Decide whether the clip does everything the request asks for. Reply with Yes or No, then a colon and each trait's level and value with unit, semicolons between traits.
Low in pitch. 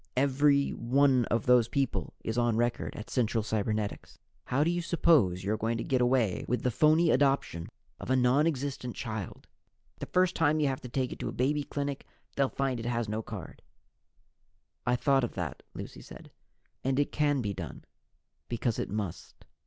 Yes: low, 125 Hz